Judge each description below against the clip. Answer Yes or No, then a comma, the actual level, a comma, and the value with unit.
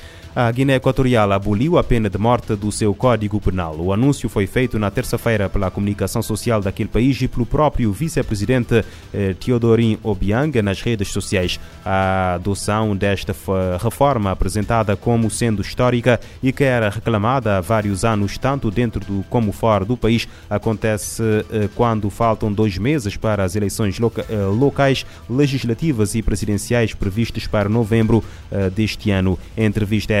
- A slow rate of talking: No, average, 145 wpm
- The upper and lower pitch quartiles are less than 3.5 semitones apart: Yes, average, 3.0 semitones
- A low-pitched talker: Yes, low, 110 Hz